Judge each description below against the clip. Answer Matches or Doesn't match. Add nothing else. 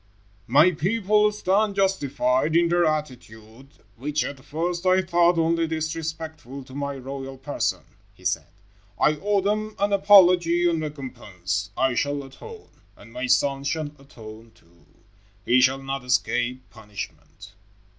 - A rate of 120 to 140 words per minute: Matches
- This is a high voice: Doesn't match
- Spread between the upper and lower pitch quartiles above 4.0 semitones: Matches